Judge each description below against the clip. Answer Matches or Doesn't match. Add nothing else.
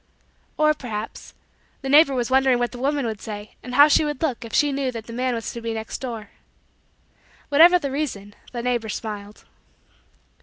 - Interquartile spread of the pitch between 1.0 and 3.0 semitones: Doesn't match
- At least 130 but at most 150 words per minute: Doesn't match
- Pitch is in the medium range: Doesn't match